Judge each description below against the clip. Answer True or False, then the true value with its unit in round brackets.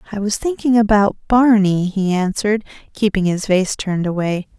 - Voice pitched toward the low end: False (200 Hz)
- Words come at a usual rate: True (155 wpm)